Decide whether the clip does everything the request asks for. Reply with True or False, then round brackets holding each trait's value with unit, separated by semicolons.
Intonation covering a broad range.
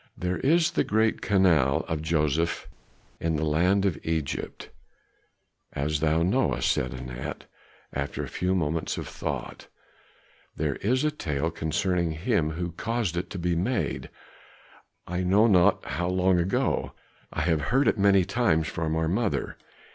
False (3.7 semitones)